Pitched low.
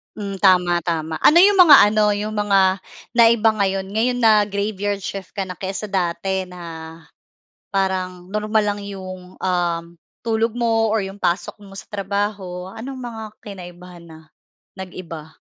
No: high, 195 Hz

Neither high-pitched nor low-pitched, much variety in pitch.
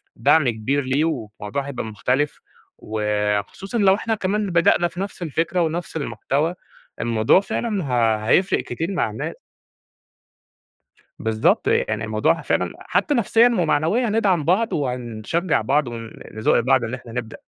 Yes: medium, 145 Hz; wide, 8.3 semitones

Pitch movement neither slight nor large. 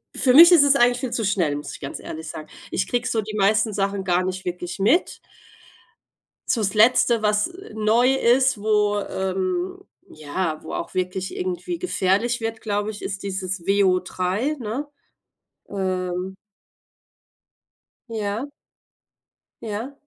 Yes: average, 4.4 semitones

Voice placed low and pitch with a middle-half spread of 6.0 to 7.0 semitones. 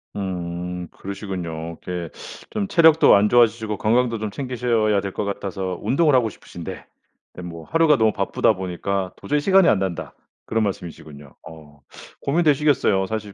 No: low, 100 Hz; wide, 5.6 semitones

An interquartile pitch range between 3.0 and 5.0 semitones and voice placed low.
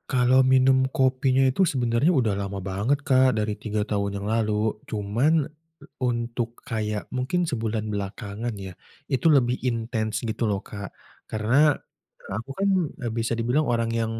Yes: average, 3.3 semitones; low, 115 Hz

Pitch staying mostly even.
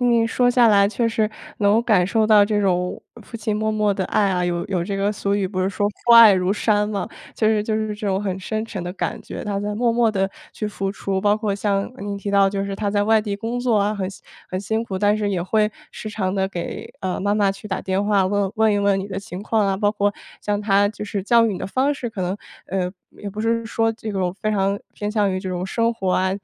Yes: narrow, 1.9 semitones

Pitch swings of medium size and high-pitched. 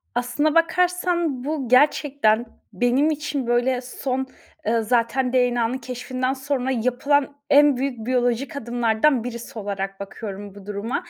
Yes: average, 3.3 semitones; very high, 250 Hz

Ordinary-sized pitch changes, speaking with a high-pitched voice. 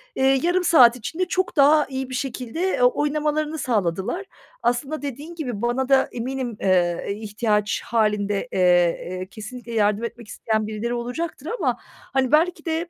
No: wide, 5.7 semitones; high, 245 Hz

